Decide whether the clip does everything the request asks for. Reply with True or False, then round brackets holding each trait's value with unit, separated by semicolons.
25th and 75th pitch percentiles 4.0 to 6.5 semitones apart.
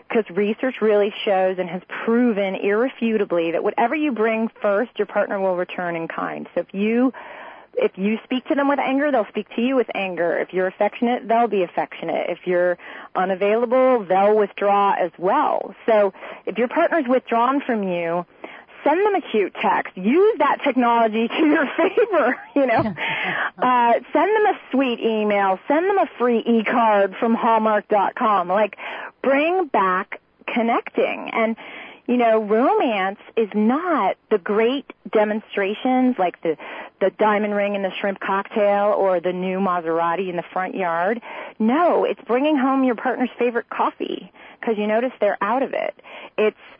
True (4.4 semitones)